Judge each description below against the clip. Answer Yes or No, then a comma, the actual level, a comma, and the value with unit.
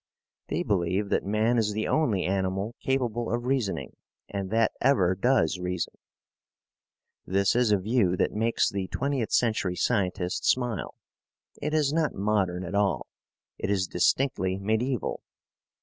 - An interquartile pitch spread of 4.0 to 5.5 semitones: Yes, average, 4.3 semitones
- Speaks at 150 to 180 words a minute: No, average, 140 wpm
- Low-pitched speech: Yes, low, 105 Hz